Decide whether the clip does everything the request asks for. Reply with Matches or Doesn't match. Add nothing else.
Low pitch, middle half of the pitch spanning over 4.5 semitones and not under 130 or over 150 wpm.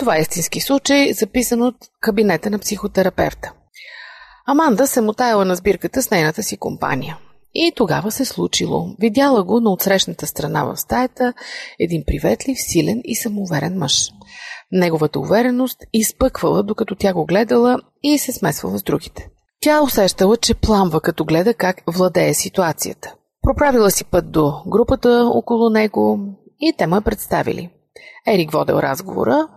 Doesn't match